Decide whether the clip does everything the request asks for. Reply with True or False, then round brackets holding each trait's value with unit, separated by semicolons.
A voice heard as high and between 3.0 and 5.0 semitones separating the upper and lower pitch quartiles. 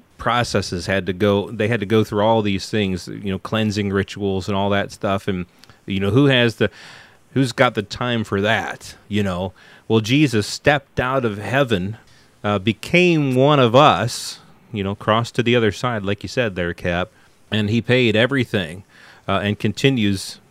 False (105 Hz; 3.3 semitones)